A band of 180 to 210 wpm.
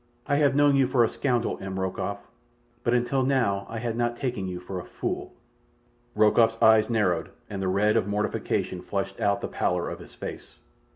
Yes: average, 190 wpm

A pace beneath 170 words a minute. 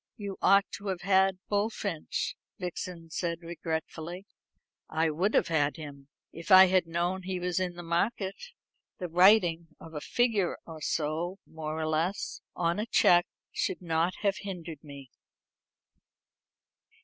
Yes: average, 145 wpm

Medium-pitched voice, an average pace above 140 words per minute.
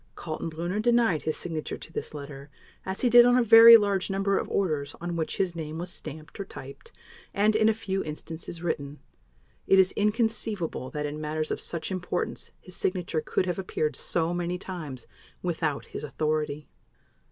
Yes: medium, 175 Hz; average, 175 wpm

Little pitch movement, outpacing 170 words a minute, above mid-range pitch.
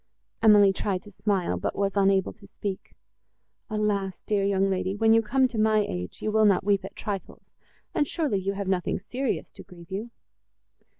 Yes: narrow, 1.9 semitones; average, 185 wpm; high, 200 Hz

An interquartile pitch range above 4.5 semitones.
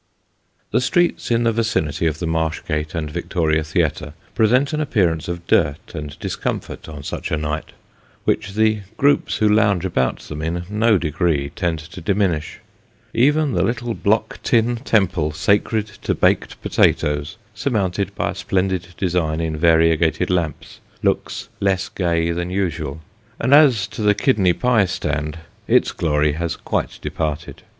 Yes: average, 5.3 semitones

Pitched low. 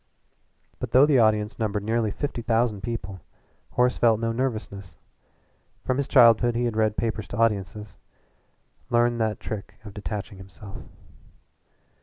Yes: low, 110 Hz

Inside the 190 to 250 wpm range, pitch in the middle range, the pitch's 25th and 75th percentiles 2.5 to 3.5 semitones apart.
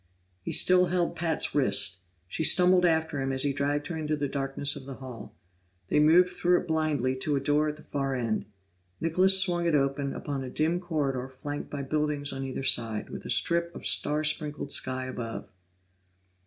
Yes: average, 195 wpm; medium, 145 Hz; average, 3.2 semitones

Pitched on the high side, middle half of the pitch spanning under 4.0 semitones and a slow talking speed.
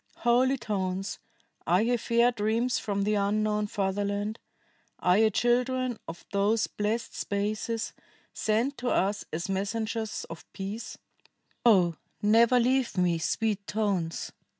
Yes: high, 215 Hz; average, 2.8 semitones; slow, 125 wpm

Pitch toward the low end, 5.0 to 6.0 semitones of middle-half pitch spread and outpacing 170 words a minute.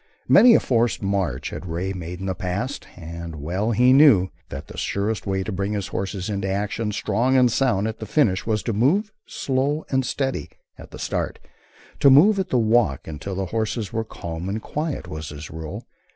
Yes: low, 105 Hz; wide, 5.4 semitones; average, 200 wpm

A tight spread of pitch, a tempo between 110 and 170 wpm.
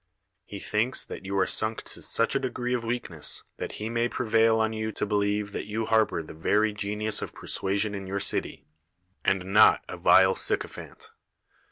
No: narrow, 2.0 semitones; average, 190 wpm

